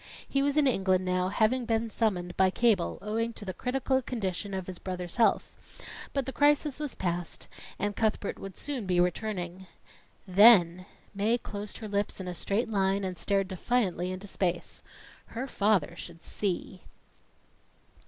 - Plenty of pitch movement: No, average, 3.9 semitones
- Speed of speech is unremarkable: Yes, average, 160 wpm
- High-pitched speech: Yes, high, 200 Hz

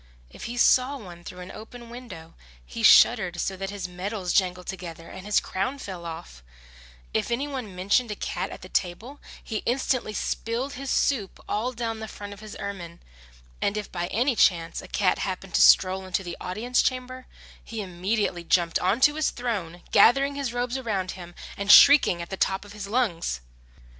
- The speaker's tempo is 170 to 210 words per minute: Yes, average, 190 wpm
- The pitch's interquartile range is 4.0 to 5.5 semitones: Yes, average, 5.2 semitones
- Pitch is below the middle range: No, high, 205 Hz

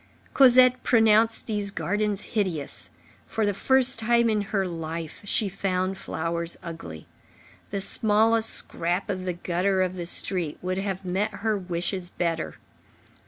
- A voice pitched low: No, high, 195 Hz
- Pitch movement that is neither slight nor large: Yes, average, 3.5 semitones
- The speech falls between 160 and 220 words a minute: No, average, 140 wpm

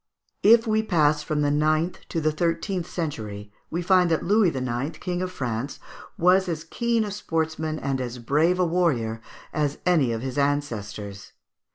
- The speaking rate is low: No, average, 175 wpm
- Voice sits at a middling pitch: Yes, medium, 155 Hz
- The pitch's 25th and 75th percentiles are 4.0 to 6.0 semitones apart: Yes, average, 5.2 semitones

